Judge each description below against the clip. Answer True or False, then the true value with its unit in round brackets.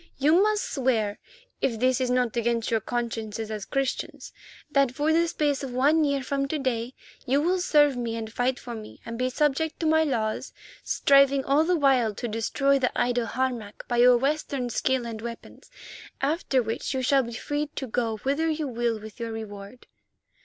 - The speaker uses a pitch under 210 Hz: False (255 Hz)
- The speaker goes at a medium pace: True (185 wpm)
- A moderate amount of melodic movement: True (3.6 semitones)